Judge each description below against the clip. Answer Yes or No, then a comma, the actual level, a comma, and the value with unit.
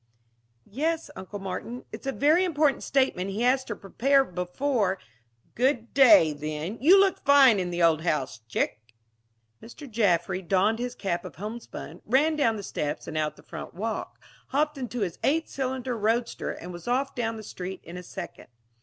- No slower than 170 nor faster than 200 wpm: Yes, average, 180 wpm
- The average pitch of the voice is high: Yes, high, 225 Hz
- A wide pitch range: Yes, wide, 6.9 semitones